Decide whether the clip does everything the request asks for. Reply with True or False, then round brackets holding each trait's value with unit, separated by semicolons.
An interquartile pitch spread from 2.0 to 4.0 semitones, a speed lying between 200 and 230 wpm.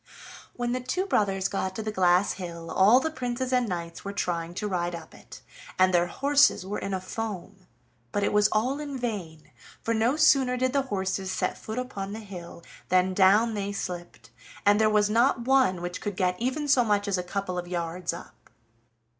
False (4.9 semitones; 205 wpm)